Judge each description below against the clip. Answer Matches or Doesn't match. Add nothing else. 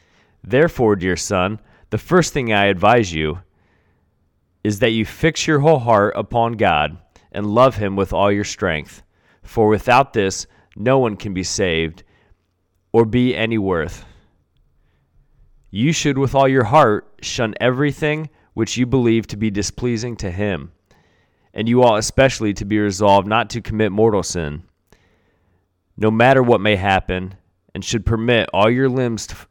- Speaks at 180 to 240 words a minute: Doesn't match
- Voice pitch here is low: Matches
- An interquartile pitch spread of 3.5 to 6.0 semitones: Matches